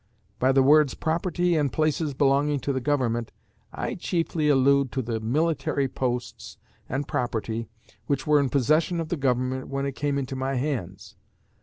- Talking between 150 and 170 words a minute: Yes, average, 165 wpm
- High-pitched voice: No, medium, 140 Hz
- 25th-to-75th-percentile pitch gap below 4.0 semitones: Yes, average, 2.8 semitones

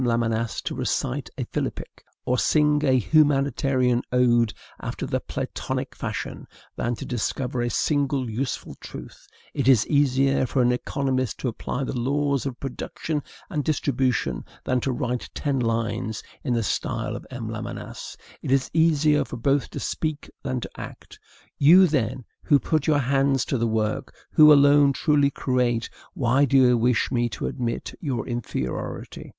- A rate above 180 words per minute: No, average, 160 wpm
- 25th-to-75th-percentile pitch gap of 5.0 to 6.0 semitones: No, average, 2.9 semitones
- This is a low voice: Yes, low, 130 Hz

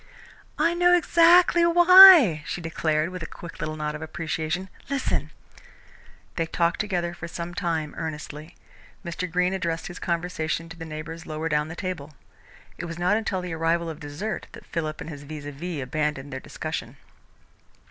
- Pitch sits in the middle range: Yes, medium, 165 Hz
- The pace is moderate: Yes, average, 170 wpm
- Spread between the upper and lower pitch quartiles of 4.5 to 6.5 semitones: No, average, 2.9 semitones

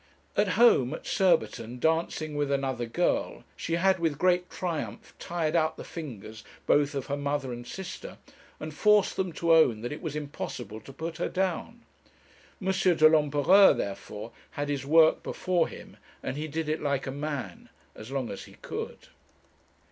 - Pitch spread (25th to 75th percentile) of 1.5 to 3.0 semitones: No, average, 4.2 semitones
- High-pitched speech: No, medium, 150 Hz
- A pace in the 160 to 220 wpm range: Yes, average, 170 wpm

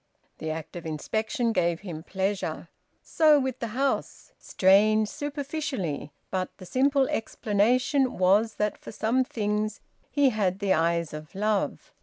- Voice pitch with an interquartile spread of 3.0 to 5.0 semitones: No, wide, 5.6 semitones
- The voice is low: No, high, 215 Hz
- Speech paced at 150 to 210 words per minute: No, average, 140 wpm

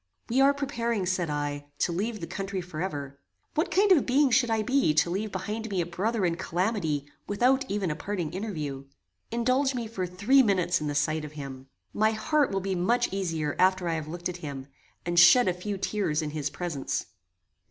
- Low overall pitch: No, medium, 185 Hz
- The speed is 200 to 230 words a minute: Yes, fast, 205 wpm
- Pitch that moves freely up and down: Yes, wide, 6.1 semitones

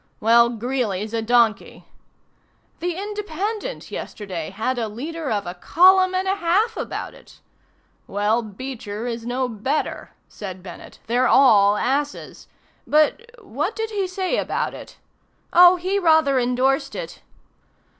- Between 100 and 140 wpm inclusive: Yes, slow, 135 wpm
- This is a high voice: Yes, very high, 260 Hz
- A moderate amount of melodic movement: No, wide, 8.5 semitones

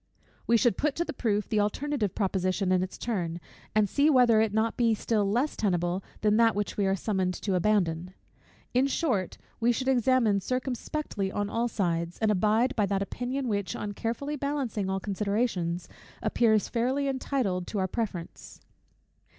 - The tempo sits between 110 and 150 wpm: No, average, 170 wpm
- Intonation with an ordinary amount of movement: Yes, average, 4.3 semitones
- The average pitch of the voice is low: No, high, 215 Hz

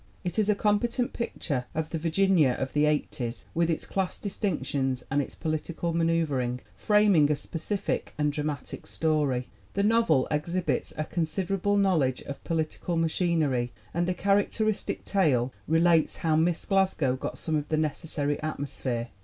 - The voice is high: No, medium, 160 Hz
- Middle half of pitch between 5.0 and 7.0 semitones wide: No, average, 4.3 semitones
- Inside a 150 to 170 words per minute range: Yes, average, 155 wpm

